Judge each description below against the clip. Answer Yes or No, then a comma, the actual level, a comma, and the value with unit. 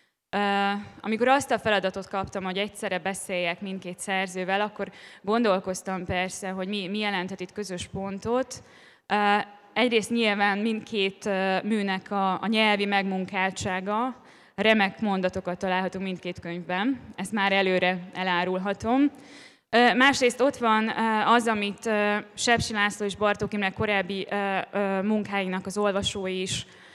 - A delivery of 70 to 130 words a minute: Yes, average, 110 wpm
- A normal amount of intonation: No, narrow, 2.3 semitones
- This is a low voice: No, high, 200 Hz